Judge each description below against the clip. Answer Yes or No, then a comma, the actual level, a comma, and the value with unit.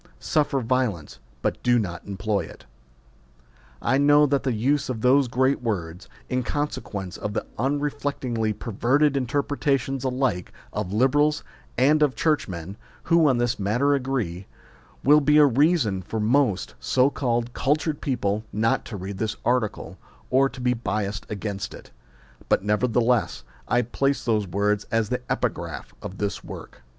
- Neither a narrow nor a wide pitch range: Yes, average, 4.8 semitones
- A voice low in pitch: Yes, low, 125 Hz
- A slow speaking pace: No, average, 155 wpm